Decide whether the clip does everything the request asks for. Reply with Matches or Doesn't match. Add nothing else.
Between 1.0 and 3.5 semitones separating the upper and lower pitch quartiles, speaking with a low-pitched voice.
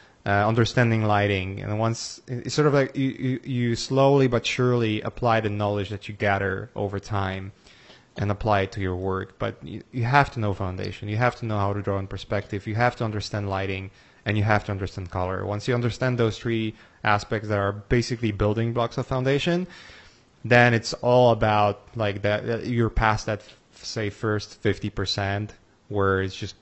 Matches